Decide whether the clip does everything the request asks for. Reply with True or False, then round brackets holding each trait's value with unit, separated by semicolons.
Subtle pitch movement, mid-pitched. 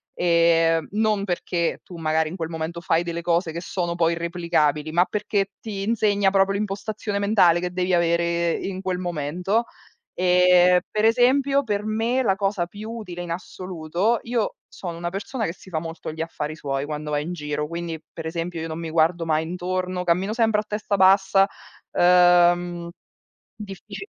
False (3.0 semitones; 180 Hz)